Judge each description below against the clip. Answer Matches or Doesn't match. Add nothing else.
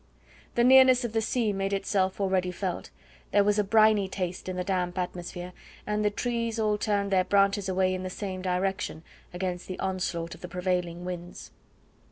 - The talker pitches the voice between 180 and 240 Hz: Matches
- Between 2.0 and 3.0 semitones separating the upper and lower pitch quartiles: Matches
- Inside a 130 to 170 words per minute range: Doesn't match